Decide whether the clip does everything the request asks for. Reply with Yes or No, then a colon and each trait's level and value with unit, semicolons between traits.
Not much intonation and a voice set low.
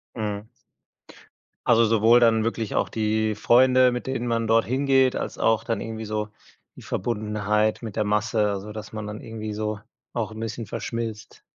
Yes: narrow, 1.6 semitones; low, 110 Hz